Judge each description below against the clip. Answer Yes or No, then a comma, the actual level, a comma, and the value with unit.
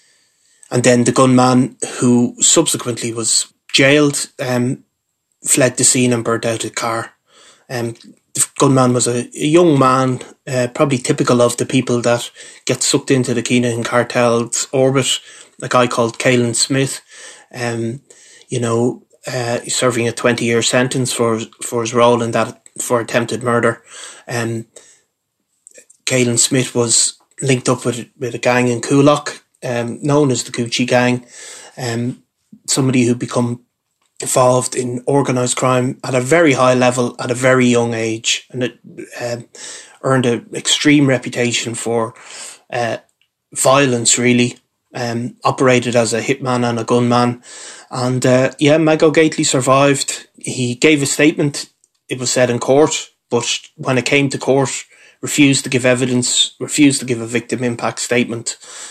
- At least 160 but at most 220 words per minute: No, average, 150 wpm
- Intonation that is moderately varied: No, narrow, 1.8 semitones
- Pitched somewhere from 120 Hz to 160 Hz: Yes, low, 125 Hz